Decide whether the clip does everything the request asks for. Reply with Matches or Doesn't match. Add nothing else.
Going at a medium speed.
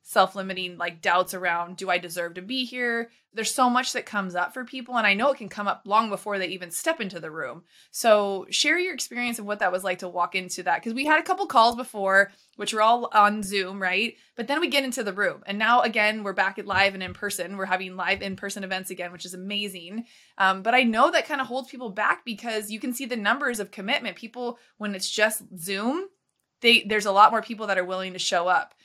Doesn't match